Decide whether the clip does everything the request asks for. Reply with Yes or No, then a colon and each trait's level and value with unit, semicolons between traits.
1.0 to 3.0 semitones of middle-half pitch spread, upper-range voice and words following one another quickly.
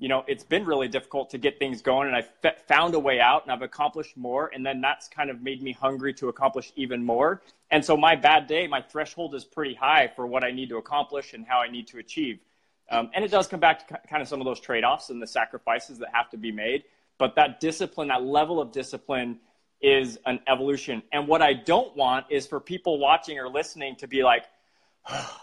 No: narrow, 2.6 semitones; low, 135 Hz; fast, 240 wpm